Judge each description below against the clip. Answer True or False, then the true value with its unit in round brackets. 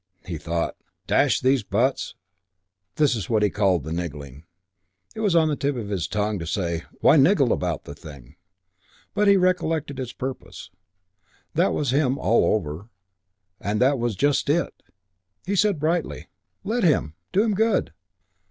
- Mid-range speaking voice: False (125 Hz)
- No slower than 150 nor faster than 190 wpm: True (160 wpm)